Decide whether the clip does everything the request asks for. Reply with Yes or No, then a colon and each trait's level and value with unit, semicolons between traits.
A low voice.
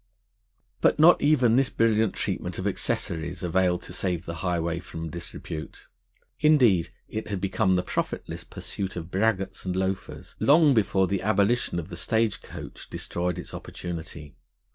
Yes: very low, 95 Hz